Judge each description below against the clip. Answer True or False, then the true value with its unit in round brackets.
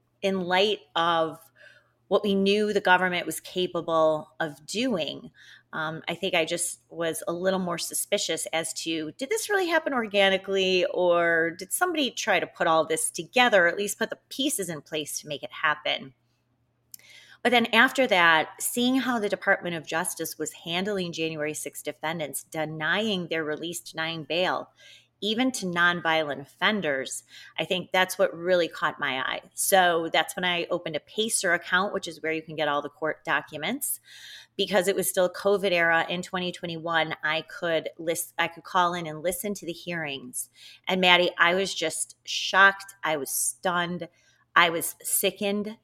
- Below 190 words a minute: True (175 wpm)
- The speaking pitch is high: False (170 Hz)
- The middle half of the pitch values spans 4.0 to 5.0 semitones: False (3.4 semitones)